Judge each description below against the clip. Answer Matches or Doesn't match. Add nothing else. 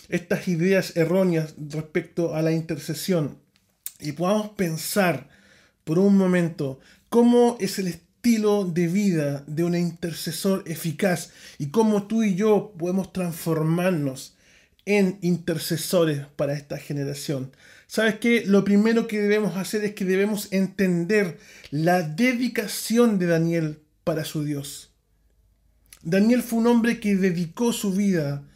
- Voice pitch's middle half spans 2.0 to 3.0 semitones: Doesn't match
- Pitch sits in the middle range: Matches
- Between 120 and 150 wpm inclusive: Matches